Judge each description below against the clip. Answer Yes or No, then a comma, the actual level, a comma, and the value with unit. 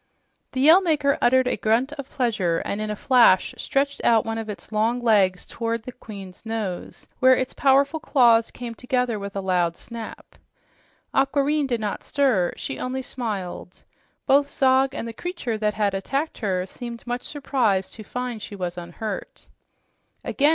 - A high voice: Yes, high, 235 Hz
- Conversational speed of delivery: Yes, average, 170 wpm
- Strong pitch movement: No, average, 4.2 semitones